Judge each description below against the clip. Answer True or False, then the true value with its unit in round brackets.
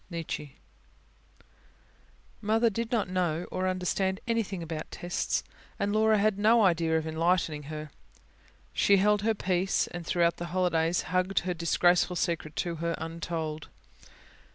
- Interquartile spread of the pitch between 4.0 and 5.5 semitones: False (3.1 semitones)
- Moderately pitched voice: True (180 Hz)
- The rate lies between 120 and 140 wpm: True (135 wpm)